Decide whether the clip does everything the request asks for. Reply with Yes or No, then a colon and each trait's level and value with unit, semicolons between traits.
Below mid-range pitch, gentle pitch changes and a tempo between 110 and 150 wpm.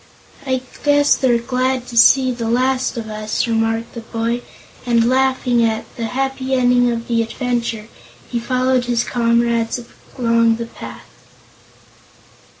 No: high, 240 Hz; narrow, 1.8 semitones; average, 140 wpm